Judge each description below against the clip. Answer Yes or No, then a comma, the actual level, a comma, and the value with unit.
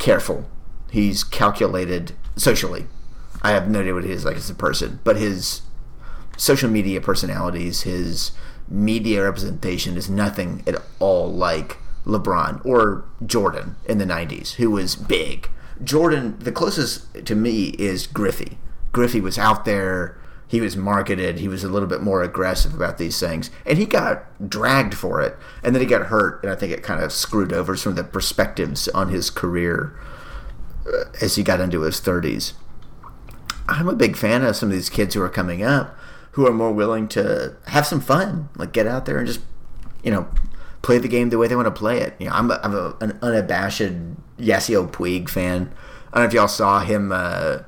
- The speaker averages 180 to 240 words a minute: Yes, average, 190 wpm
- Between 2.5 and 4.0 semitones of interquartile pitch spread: No, average, 4.8 semitones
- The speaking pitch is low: Yes, low, 105 Hz